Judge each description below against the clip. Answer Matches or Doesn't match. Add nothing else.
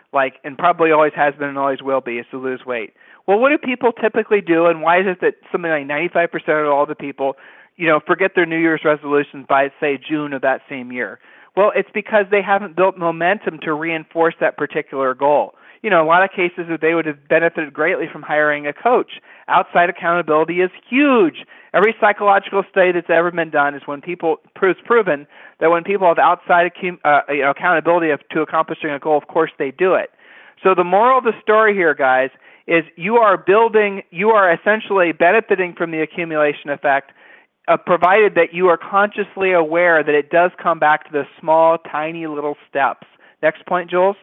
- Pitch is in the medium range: Matches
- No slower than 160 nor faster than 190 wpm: Doesn't match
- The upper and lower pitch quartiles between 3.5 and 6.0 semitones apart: Matches